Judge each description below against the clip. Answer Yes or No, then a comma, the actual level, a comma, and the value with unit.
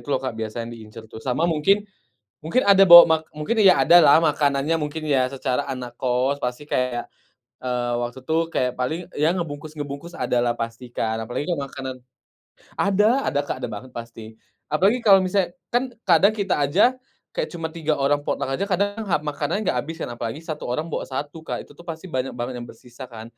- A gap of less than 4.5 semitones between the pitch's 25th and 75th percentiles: No, wide, 5.5 semitones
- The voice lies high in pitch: No, medium, 145 Hz